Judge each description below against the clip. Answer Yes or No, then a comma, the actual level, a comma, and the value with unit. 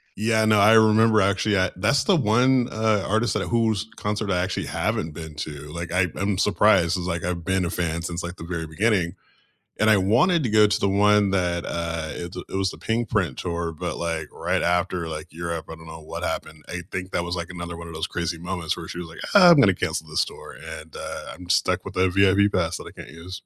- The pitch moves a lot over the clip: No, average, 3.8 semitones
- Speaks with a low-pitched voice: Yes, very low, 90 Hz